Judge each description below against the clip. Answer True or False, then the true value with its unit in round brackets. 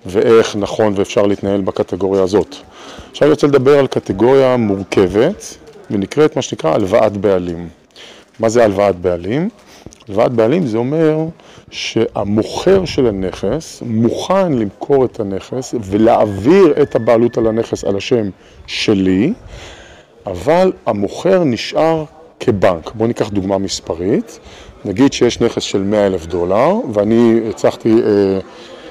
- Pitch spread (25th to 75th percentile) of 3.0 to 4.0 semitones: False (5.6 semitones)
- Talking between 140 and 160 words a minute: False (120 wpm)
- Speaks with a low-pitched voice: True (115 Hz)